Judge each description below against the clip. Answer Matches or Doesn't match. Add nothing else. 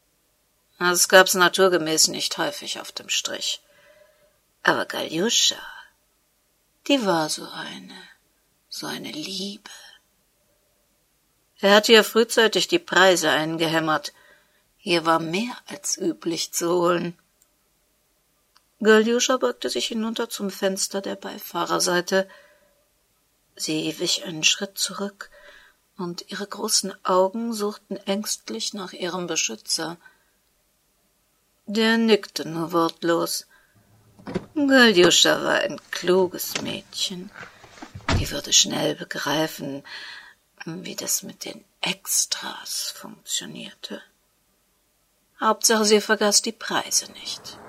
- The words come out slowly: Matches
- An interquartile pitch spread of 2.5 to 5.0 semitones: Matches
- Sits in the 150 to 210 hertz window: Matches